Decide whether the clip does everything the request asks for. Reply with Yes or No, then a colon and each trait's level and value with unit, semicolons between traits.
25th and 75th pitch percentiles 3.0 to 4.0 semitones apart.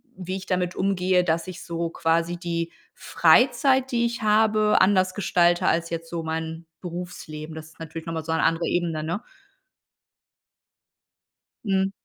No: narrow, 2.5 semitones